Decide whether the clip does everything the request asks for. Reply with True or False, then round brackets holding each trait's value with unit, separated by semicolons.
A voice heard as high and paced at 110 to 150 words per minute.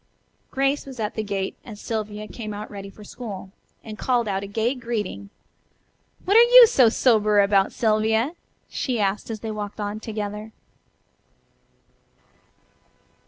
True (215 Hz; 145 wpm)